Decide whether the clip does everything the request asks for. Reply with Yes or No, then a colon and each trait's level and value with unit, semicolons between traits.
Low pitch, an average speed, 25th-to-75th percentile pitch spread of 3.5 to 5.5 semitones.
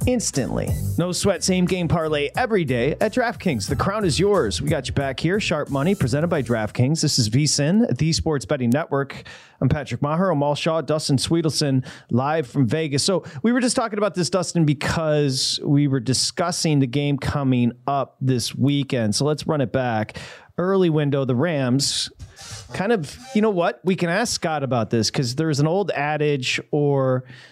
No: medium, 145 Hz; average, 190 wpm; average, 4.0 semitones